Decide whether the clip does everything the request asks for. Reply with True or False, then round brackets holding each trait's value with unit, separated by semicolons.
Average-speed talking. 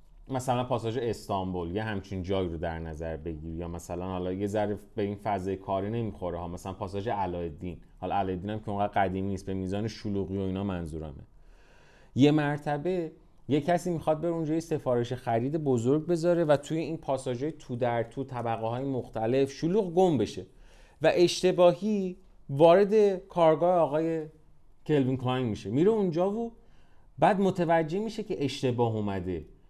False (160 wpm)